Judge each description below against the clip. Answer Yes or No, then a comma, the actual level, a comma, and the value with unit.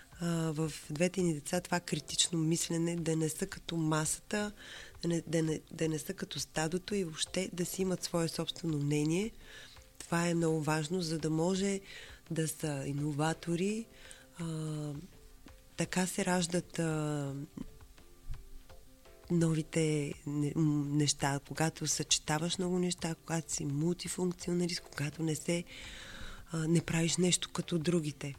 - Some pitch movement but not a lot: No, narrow, 2.3 semitones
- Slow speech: No, average, 130 wpm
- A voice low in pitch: No, medium, 165 Hz